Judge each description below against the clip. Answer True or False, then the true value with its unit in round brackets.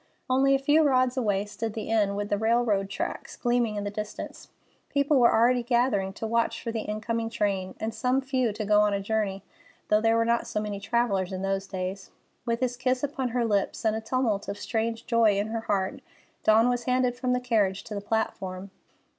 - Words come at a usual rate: False (210 wpm)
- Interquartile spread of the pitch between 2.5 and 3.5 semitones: True (3.1 semitones)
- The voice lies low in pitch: False (225 Hz)